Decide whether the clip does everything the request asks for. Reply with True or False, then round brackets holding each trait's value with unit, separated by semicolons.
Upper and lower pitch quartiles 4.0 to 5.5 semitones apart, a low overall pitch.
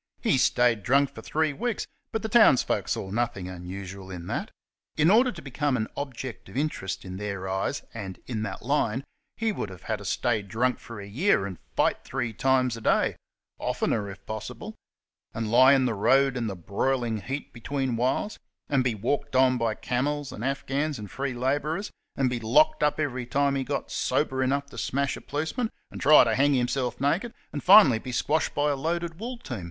True (4.6 semitones; 130 Hz)